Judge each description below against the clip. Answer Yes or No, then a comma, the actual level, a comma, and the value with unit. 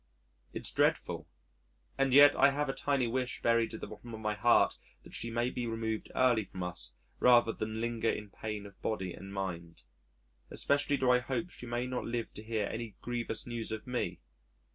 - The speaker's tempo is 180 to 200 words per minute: Yes, average, 195 wpm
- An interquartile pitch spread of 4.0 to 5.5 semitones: No, average, 2.7 semitones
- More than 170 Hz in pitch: No, low, 115 Hz